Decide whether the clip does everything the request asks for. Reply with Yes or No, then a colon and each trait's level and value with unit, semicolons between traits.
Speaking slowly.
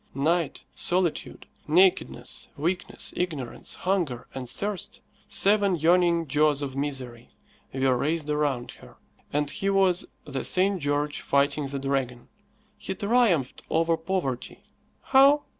Yes: slow, 120 wpm